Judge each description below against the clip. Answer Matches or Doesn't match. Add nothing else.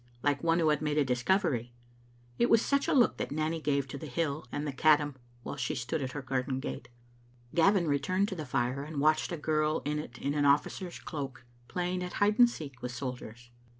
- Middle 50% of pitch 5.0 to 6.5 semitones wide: Doesn't match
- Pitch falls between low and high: Matches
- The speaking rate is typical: Doesn't match